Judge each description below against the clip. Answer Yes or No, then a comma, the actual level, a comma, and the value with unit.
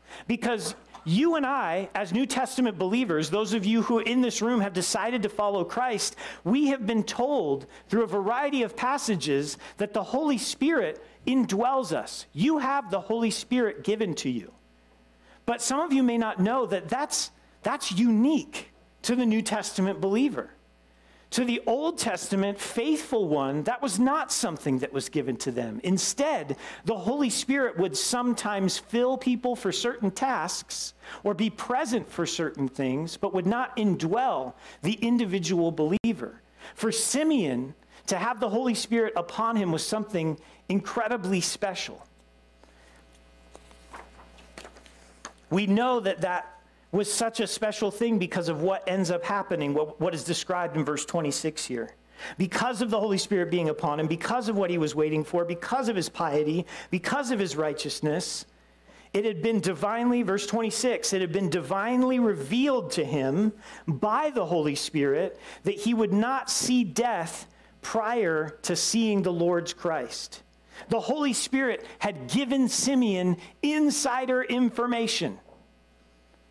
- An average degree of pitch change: No, wide, 6.5 semitones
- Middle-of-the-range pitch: No, high, 205 Hz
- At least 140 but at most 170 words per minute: Yes, average, 150 wpm